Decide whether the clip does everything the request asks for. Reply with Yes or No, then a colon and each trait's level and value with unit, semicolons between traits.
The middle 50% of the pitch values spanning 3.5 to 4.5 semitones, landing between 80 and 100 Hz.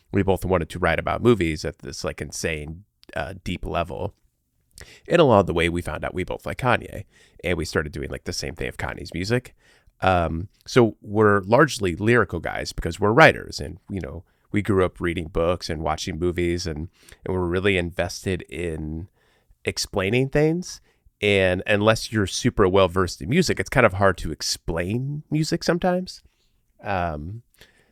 Yes: average, 4.1 semitones; very low, 95 Hz